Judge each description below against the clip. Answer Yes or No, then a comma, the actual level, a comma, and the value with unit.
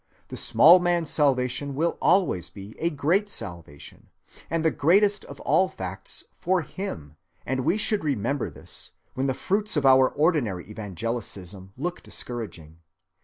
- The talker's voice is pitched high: No, low, 135 Hz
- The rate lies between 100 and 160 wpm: Yes, average, 145 wpm